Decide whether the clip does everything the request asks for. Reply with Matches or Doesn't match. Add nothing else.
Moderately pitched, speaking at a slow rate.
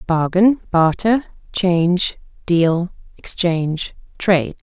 Matches